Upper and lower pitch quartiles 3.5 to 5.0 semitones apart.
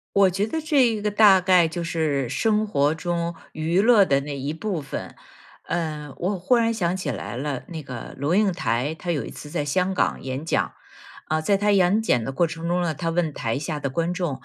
Yes: average, 4.6 semitones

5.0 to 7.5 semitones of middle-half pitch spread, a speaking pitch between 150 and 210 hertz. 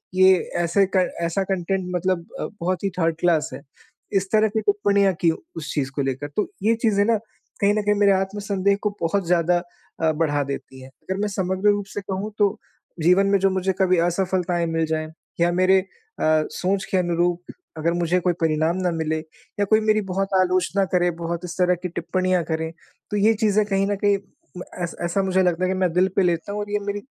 No: average, 2.8 semitones; medium, 185 Hz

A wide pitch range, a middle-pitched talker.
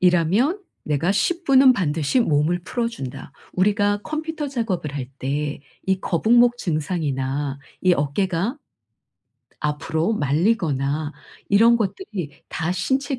Yes: wide, 7.7 semitones; medium, 180 Hz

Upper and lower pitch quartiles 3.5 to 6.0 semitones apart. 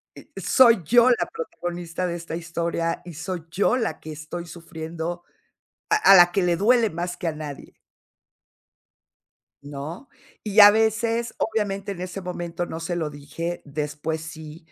Yes: average, 4.0 semitones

